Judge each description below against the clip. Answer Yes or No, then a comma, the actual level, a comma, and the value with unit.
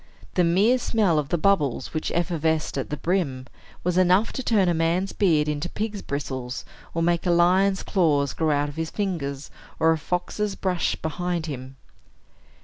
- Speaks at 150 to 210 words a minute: Yes, average, 175 wpm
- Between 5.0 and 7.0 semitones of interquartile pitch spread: No, average, 3.9 semitones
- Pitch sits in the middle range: Yes, medium, 170 Hz